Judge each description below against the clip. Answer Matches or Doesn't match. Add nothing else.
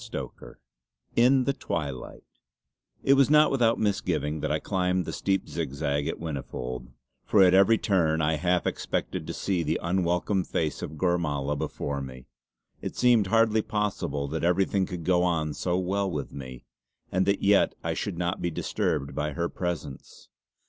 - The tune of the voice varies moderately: Matches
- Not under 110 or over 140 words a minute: Doesn't match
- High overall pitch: Doesn't match